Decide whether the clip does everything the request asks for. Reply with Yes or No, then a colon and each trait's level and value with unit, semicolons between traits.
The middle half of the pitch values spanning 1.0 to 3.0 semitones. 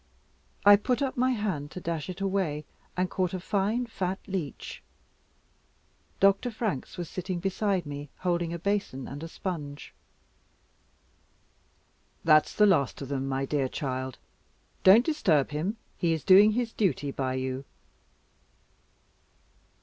No: wide, 5.6 semitones